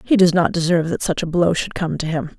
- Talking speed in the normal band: No, fast, 300 wpm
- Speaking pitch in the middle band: Yes, medium, 170 Hz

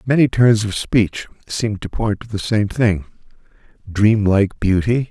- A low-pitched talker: Yes, low, 105 Hz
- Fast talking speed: No, average, 140 wpm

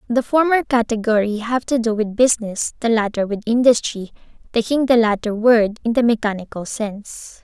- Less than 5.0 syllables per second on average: No, 5.3 syllables/s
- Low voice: No, high, 225 Hz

